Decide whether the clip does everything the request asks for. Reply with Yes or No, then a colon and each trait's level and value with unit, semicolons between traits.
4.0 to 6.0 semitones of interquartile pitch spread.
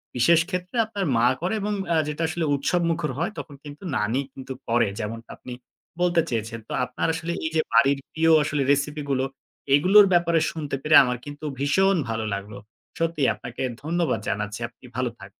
Yes: average, 5.2 semitones